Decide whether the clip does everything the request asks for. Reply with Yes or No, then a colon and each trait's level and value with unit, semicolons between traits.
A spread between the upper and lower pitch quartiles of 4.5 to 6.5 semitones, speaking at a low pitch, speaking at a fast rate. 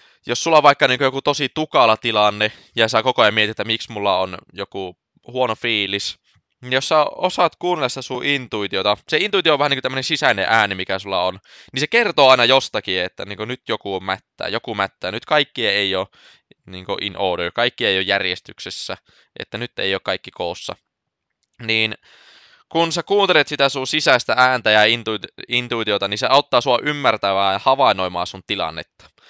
Yes: wide, 5.4 semitones; low, 120 Hz; fast, 185 wpm